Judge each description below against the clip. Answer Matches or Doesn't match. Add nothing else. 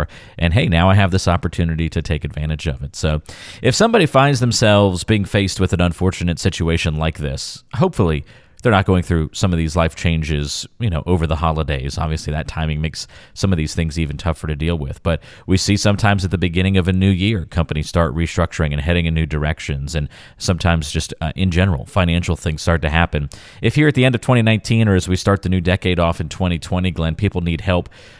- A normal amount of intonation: Matches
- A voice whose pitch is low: Matches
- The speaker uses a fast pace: Matches